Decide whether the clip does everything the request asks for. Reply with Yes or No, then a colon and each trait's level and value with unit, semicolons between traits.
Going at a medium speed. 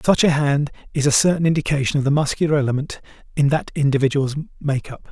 Yes: average, 175 wpm